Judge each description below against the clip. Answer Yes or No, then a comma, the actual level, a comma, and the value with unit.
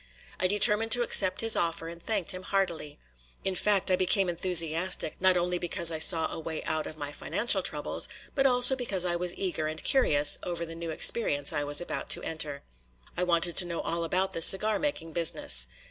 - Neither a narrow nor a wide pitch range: Yes, average, 3.0 semitones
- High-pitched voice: No, medium, 175 Hz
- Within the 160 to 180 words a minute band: No, fast, 205 wpm